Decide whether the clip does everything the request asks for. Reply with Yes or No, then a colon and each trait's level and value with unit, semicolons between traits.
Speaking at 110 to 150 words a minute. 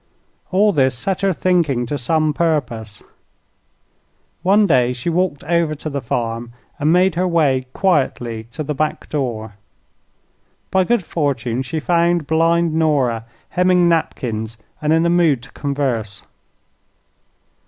Yes: slow, 135 wpm